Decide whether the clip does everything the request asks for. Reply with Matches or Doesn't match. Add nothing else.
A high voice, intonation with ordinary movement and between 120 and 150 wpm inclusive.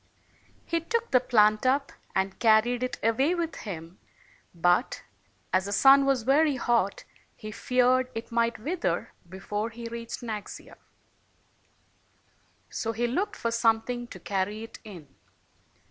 Matches